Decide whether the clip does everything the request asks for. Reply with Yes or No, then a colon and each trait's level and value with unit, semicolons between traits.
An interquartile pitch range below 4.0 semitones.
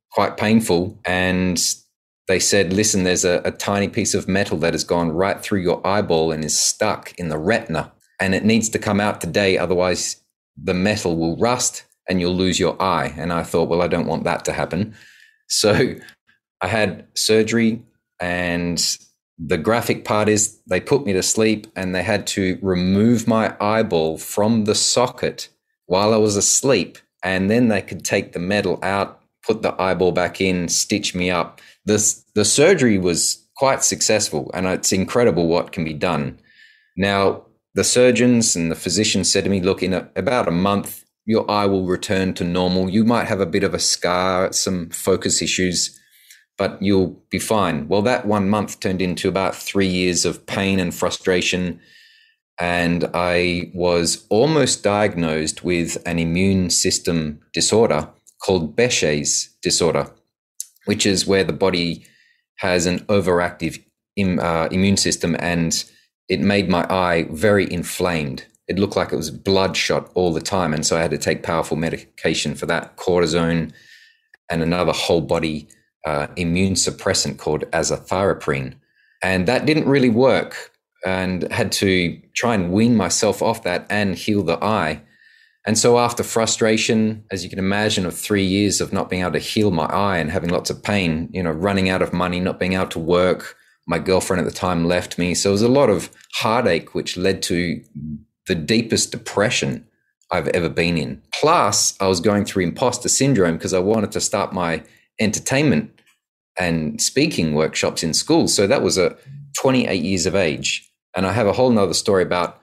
Yes: average, 3.2 semitones